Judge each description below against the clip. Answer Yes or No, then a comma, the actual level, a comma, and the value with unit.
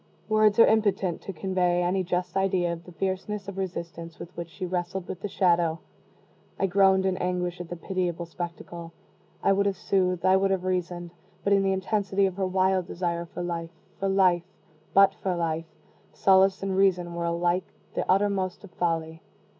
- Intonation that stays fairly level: Yes, narrow, 1.9 semitones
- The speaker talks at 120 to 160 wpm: No, average, 185 wpm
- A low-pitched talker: No, medium, 185 Hz